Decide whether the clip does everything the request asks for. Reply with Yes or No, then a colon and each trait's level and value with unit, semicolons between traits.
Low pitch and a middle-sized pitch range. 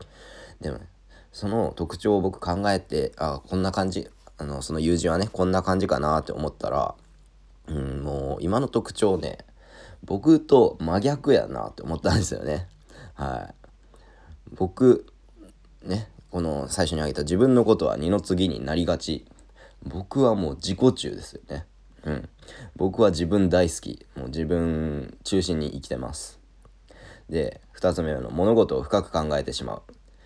Yes: very low, 85 Hz; average, 3.9 semitones